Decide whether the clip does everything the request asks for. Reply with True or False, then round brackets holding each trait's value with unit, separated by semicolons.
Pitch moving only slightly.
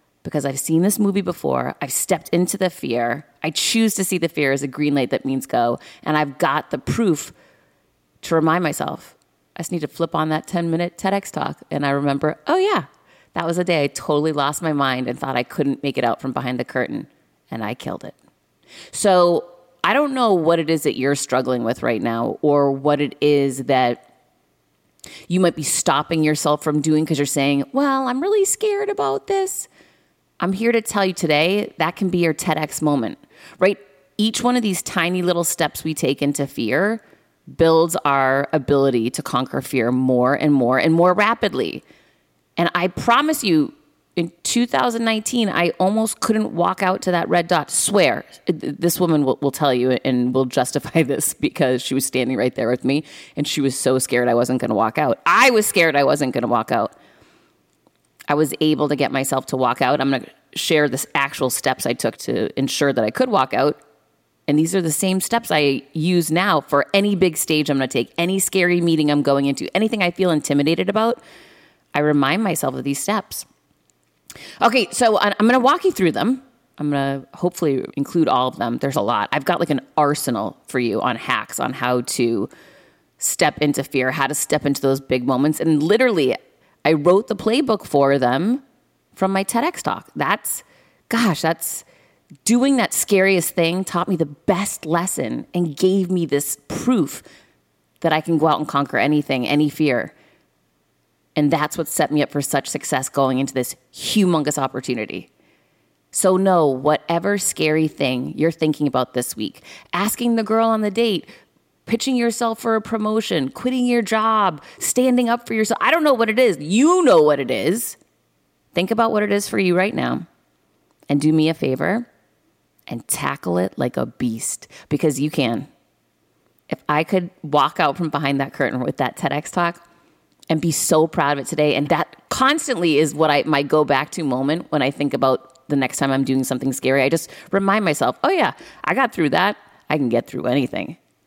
False (5.5 semitones)